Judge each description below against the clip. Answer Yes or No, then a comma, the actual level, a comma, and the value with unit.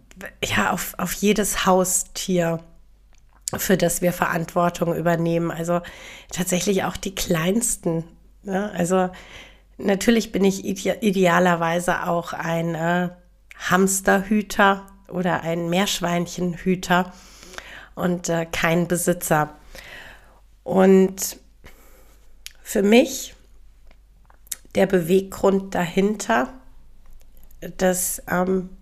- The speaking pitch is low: No, medium, 180 Hz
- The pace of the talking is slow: Yes, slow, 85 wpm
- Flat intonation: Yes, narrow, 2.0 semitones